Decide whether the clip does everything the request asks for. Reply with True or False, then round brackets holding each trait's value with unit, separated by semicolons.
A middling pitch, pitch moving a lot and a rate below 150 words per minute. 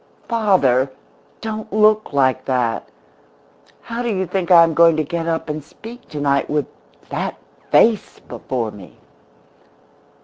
True (165 Hz; 7.4 semitones; 135 wpm)